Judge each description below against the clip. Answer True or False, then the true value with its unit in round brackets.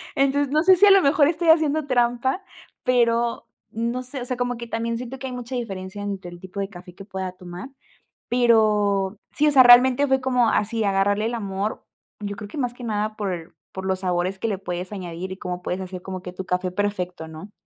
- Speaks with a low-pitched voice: False (215 Hz)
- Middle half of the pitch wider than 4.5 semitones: True (4.9 semitones)